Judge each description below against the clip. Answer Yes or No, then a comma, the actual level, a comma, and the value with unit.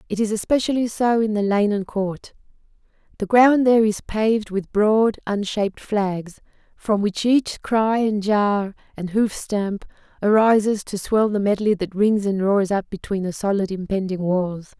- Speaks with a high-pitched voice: Yes, high, 205 Hz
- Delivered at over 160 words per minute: Yes, average, 170 wpm